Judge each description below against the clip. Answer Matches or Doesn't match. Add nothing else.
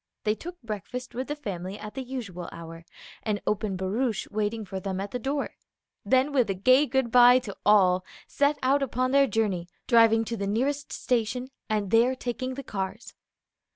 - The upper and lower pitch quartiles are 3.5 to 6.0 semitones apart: Matches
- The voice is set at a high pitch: Matches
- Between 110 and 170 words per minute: Doesn't match